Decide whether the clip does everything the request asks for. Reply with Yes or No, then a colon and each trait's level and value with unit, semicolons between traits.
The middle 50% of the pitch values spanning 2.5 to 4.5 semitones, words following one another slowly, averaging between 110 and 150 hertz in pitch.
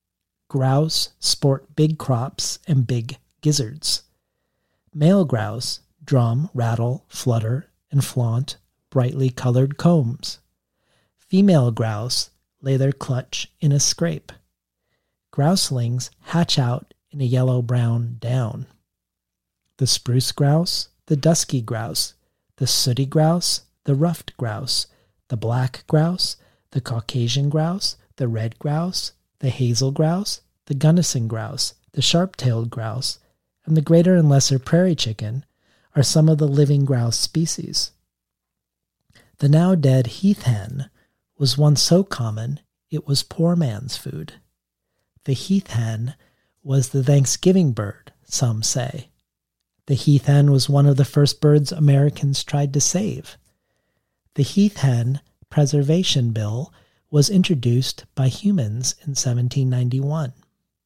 Yes: average, 4.1 semitones; slow, 125 wpm; low, 135 Hz